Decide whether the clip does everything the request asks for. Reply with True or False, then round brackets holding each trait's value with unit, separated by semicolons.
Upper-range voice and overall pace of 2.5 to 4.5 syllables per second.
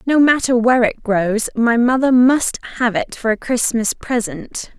True (240 Hz; 4.4 syllables/s)